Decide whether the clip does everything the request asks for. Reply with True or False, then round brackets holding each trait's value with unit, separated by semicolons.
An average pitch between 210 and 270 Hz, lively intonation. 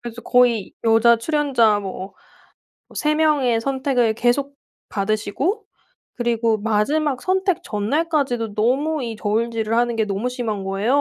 False (235 Hz; 4.4 semitones)